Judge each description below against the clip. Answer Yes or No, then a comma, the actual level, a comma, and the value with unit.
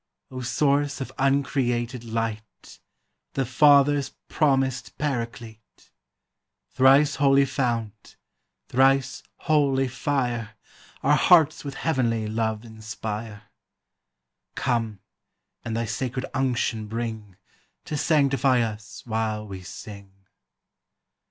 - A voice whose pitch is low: Yes, low, 125 Hz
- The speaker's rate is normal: No, slow, 95 wpm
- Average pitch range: Yes, average, 3.6 semitones